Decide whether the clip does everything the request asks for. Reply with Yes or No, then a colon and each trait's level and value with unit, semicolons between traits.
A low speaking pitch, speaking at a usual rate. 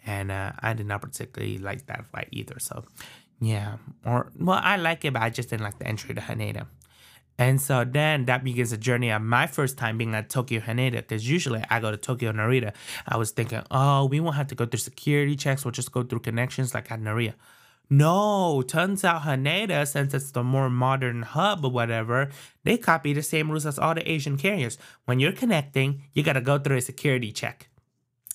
No: low, 130 Hz; fast, 215 wpm